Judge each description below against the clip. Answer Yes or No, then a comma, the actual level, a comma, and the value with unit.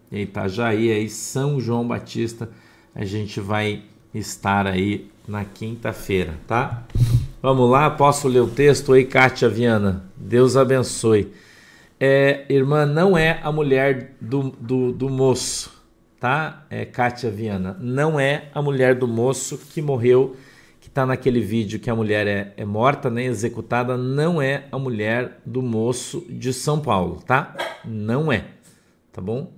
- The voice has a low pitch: Yes, low, 120 Hz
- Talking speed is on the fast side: No, average, 150 wpm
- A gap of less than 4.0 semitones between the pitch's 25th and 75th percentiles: Yes, average, 3.5 semitones